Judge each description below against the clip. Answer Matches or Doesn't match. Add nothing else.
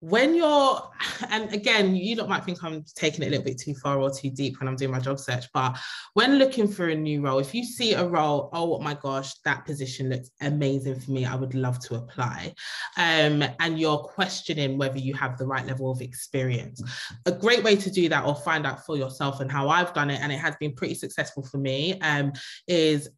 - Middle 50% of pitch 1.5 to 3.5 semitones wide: Doesn't match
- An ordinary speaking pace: Doesn't match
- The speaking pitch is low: Doesn't match